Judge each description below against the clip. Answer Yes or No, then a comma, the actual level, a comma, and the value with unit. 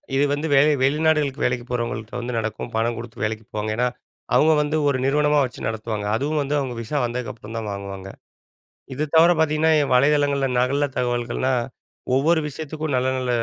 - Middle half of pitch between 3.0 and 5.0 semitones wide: Yes, average, 4.2 semitones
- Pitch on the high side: No, low, 130 Hz